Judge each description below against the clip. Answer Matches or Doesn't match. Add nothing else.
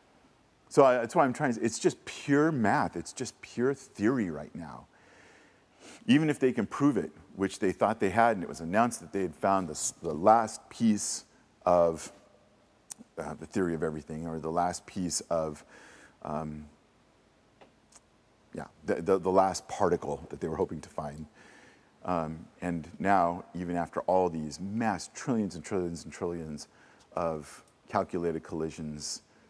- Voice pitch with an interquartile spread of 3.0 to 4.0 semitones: Matches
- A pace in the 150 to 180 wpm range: Matches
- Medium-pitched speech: Doesn't match